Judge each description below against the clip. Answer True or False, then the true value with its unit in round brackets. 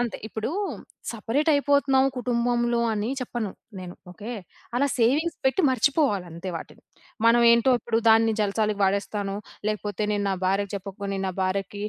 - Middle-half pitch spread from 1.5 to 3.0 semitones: False (3.4 semitones)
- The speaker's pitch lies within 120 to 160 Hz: False (225 Hz)